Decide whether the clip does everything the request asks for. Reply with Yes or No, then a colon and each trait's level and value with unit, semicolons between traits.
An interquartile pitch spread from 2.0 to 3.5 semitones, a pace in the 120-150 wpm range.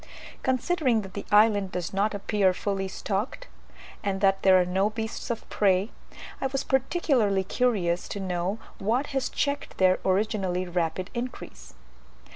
No: average, 4.1 semitones; average, 145 wpm